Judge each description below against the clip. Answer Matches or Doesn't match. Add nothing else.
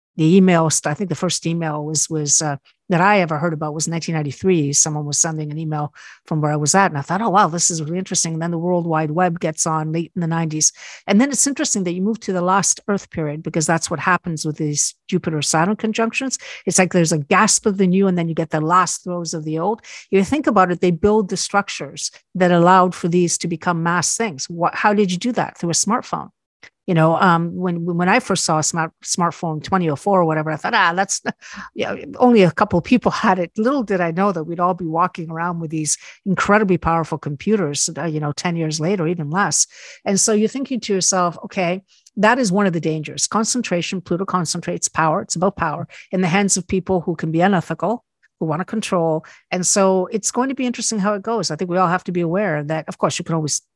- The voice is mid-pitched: Matches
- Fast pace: Matches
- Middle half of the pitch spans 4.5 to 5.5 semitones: Doesn't match